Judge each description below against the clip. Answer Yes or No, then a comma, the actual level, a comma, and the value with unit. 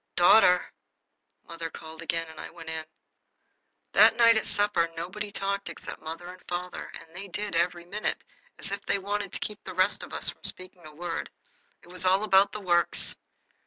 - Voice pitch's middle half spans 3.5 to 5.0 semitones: No, average, 2.9 semitones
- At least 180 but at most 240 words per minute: Yes, average, 190 wpm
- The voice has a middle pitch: Yes, medium, 180 Hz